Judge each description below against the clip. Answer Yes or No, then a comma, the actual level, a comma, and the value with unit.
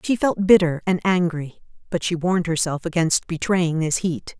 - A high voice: No, medium, 170 Hz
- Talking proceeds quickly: No, average, 175 wpm